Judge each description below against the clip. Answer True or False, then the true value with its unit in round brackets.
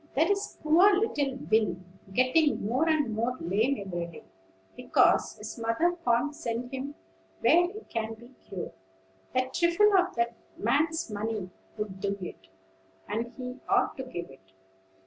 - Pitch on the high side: True (245 Hz)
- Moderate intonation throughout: False (6.5 semitones)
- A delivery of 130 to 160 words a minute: True (150 wpm)